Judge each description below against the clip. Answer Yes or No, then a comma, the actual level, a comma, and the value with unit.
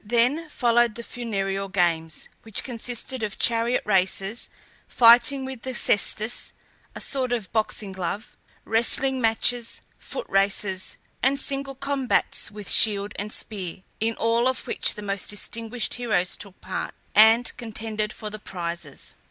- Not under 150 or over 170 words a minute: No, average, 140 wpm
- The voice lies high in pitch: Yes, high, 225 Hz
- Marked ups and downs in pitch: No, average, 3.4 semitones